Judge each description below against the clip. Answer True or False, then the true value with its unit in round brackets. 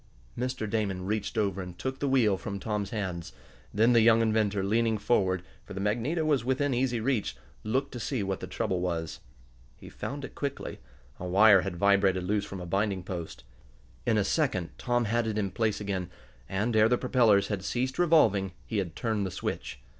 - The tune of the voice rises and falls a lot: False (3.7 semitones)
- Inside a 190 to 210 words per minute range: True (195 wpm)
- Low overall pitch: True (105 Hz)